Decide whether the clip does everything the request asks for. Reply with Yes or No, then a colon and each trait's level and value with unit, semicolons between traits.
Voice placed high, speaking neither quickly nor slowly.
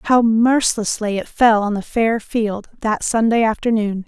Yes: high, 220 Hz; average, 160 wpm